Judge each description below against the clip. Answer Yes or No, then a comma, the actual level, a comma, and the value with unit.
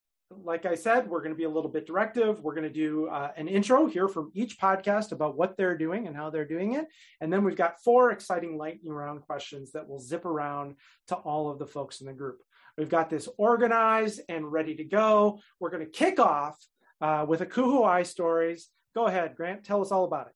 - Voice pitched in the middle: Yes, medium, 170 Hz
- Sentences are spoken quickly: Yes, fast, 230 wpm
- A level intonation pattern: No, average, 4.6 semitones